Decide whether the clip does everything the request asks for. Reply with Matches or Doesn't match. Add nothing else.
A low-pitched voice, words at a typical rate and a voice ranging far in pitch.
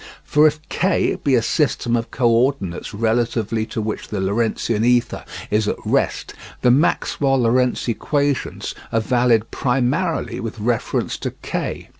Doesn't match